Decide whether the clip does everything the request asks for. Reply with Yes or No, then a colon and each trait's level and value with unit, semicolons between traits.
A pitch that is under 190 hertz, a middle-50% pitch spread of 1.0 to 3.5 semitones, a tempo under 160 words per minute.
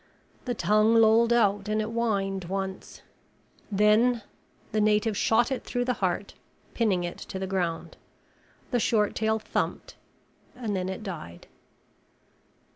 No: high, 210 Hz; average, 2.9 semitones; slow, 135 wpm